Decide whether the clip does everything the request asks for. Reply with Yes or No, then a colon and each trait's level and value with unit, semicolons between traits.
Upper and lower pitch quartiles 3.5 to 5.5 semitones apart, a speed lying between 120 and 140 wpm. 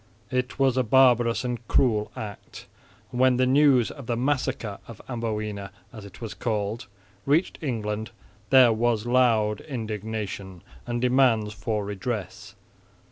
No: average, 3.1 semitones; slow, 135 wpm